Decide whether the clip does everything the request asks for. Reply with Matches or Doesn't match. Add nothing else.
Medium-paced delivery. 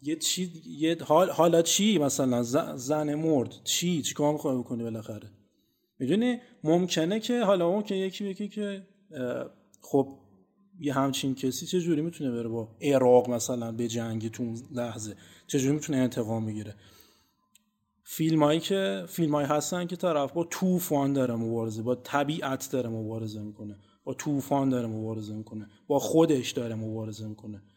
Matches